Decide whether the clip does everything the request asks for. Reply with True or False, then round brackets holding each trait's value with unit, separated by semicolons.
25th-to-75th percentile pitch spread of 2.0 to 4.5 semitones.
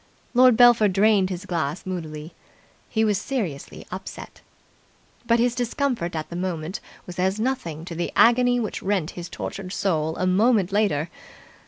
False (5.2 semitones)